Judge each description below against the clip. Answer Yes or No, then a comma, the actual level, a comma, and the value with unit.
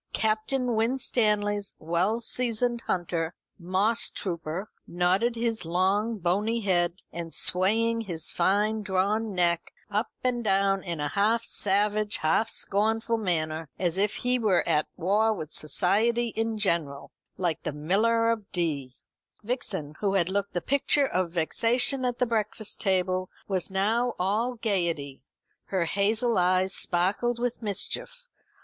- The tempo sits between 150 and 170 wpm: No, slow, 135 wpm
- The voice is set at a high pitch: Yes, high, 200 Hz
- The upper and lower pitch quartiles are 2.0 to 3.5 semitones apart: No, average, 4.3 semitones